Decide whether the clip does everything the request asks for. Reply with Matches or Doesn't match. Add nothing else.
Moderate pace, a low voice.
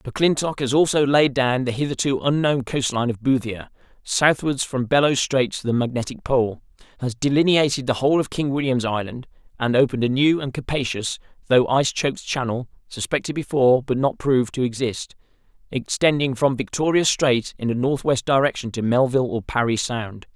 Matches